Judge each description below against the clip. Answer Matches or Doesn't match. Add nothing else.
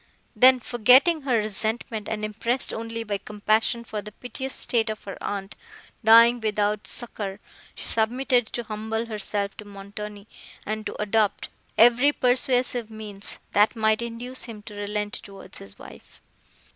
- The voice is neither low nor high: Doesn't match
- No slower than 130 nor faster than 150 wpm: Matches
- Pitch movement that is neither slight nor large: Doesn't match